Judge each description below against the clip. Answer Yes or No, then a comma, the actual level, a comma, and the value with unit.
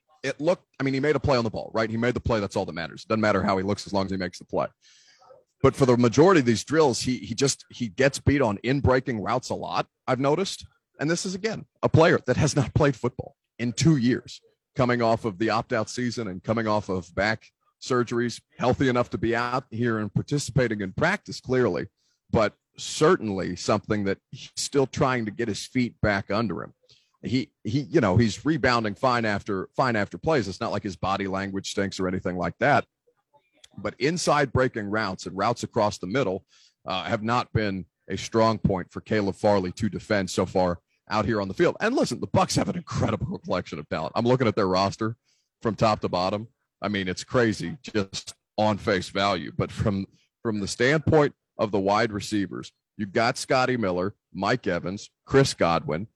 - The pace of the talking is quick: Yes, fast, 210 wpm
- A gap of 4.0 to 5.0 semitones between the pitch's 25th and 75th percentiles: Yes, average, 4.5 semitones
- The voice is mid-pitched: No, low, 115 Hz